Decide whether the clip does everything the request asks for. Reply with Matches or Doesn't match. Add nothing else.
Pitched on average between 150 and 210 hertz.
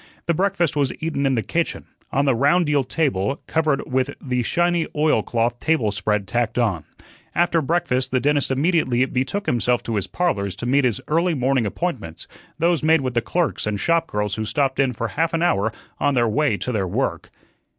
Doesn't match